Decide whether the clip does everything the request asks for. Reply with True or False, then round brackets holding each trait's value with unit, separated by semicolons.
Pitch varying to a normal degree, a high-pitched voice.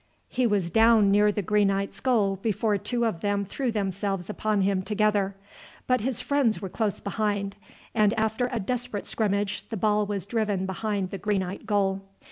False (2.0 semitones; 205 Hz)